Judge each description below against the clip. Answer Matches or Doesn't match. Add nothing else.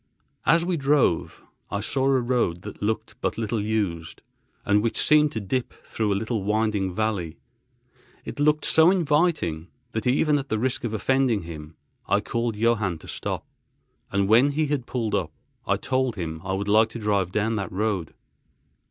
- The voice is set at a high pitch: Doesn't match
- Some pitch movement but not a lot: Matches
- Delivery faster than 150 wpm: Matches